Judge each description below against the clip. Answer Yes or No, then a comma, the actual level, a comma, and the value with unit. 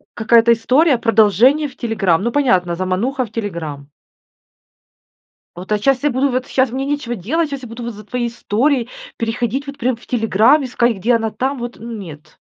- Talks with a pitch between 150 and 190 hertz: No, high, 235 Hz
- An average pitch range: Yes, average, 3.5 semitones